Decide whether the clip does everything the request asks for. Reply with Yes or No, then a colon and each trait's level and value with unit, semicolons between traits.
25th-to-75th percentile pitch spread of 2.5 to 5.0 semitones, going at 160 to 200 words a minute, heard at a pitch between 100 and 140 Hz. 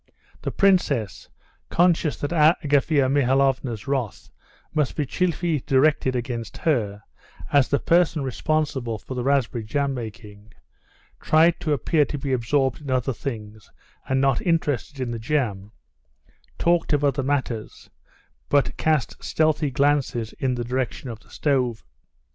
No: average, 3.8 semitones; slow, 135 wpm; low, 135 Hz